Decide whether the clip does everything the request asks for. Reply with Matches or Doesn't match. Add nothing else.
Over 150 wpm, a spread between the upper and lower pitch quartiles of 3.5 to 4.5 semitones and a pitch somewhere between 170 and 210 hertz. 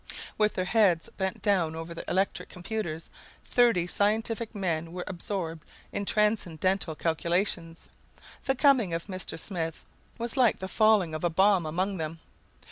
Doesn't match